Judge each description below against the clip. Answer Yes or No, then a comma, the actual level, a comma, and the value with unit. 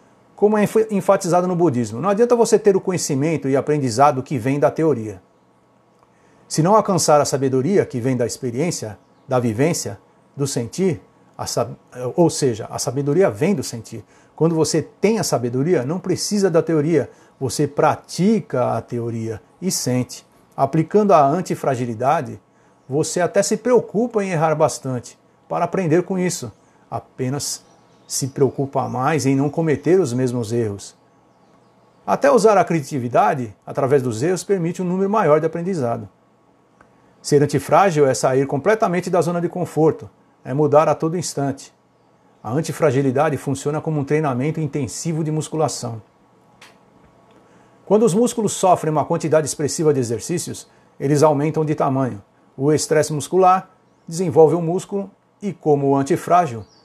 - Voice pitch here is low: No, medium, 150 Hz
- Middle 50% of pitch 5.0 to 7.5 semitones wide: No, average, 4.5 semitones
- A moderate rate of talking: Yes, average, 145 wpm